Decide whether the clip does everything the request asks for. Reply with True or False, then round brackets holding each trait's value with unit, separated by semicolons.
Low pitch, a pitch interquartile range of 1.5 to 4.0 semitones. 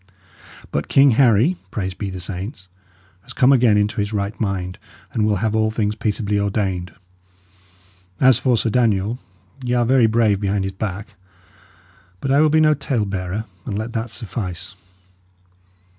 True (110 Hz; 3.5 semitones)